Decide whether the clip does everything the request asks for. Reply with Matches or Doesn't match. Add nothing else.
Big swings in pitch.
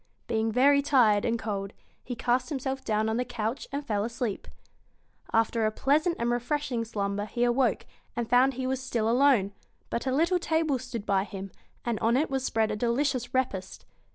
Doesn't match